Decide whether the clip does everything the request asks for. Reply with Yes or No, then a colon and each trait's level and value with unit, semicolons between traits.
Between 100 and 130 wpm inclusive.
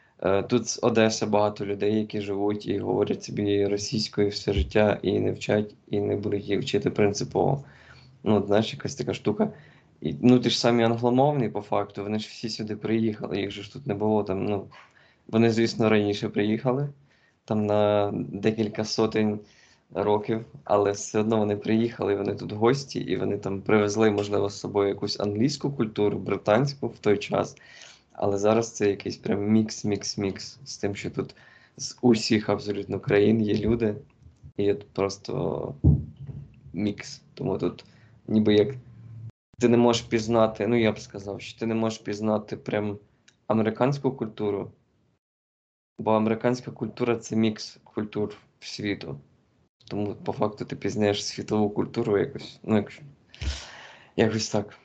No: fast, 155 wpm